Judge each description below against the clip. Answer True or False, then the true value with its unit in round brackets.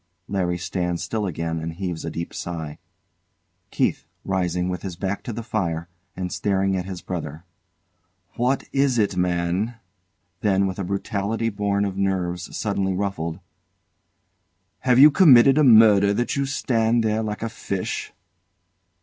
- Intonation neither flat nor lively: True (4.0 semitones)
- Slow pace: False (150 wpm)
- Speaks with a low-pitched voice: True (95 Hz)